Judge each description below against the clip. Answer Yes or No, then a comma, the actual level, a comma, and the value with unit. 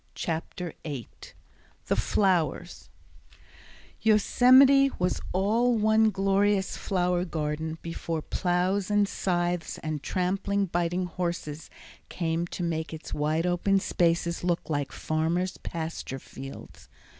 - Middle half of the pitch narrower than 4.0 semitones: Yes, average, 3.3 semitones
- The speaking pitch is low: No, medium, 175 Hz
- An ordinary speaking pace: No, slow, 110 wpm